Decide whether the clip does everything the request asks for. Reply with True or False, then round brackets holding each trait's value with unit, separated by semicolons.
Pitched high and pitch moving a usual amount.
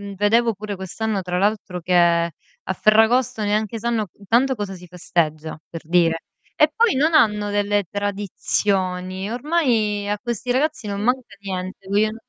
True (205 Hz; 3.5 semitones)